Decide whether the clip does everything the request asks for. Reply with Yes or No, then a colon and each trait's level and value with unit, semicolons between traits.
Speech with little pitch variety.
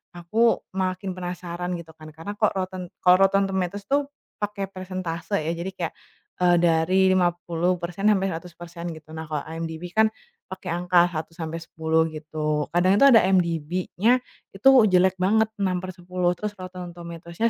Yes: narrow, 2.2 semitones